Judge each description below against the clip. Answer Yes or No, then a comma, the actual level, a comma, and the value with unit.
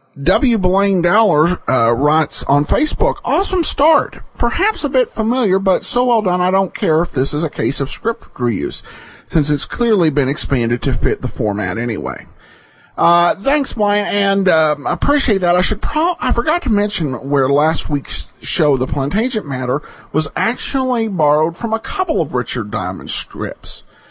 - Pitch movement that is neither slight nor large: No, wide, 7.7 semitones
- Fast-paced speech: No, average, 175 wpm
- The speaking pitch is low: No, medium, 175 Hz